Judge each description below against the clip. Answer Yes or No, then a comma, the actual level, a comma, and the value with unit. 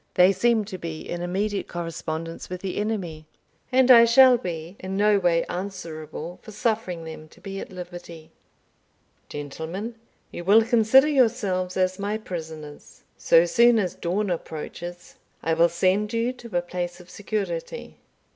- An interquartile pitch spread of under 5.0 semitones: Yes, average, 4.0 semitones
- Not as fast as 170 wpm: Yes, average, 155 wpm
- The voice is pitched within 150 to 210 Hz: Yes, medium, 185 Hz